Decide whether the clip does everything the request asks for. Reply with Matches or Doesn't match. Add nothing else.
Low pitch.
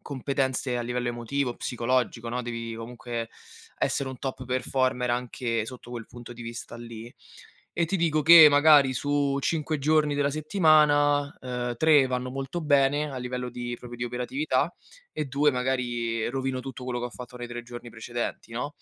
Matches